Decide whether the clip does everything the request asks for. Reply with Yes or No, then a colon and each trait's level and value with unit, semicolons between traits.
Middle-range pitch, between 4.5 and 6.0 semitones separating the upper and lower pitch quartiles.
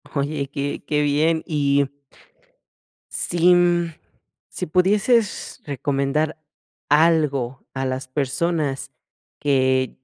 No: medium, 145 Hz; average, 3.3 semitones